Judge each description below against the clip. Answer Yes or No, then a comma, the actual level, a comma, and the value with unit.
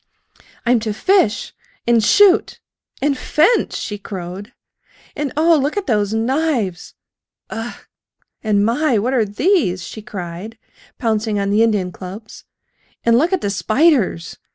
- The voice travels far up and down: Yes, wide, 6.0 semitones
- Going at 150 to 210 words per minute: No, average, 140 wpm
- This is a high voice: Yes, high, 225 Hz